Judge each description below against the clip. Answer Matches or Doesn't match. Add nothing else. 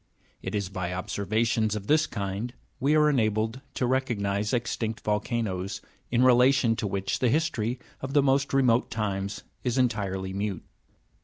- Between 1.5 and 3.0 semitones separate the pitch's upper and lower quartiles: Doesn't match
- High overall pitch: Doesn't match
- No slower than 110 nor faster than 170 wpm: Matches